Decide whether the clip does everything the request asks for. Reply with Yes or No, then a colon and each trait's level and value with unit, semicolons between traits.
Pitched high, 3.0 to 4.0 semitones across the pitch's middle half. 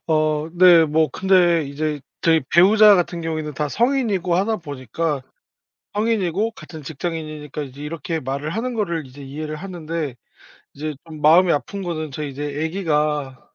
No: medium, 160 Hz; average, 3.3 semitones